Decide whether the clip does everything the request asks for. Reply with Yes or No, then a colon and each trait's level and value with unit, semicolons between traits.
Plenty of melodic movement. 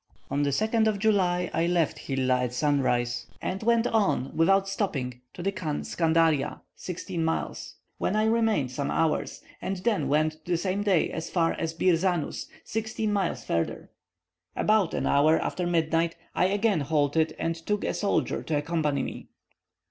No: average, 4.8 semitones